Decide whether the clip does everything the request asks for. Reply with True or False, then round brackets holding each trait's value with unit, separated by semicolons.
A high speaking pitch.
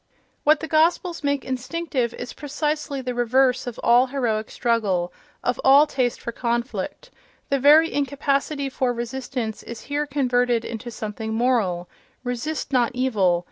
True (255 Hz)